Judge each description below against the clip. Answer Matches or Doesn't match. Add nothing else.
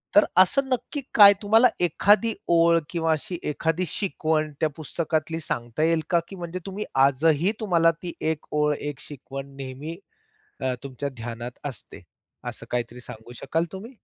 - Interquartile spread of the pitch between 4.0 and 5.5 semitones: Matches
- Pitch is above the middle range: Doesn't match